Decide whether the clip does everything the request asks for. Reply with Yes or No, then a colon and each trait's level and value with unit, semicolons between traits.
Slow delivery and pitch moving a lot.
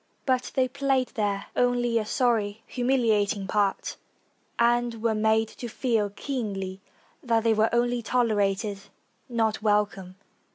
No: slow, 125 wpm; average, 2.8 semitones